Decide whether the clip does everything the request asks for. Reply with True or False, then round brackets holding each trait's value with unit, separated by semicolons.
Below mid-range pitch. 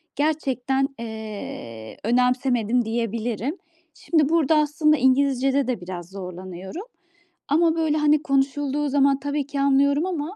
False (270 Hz)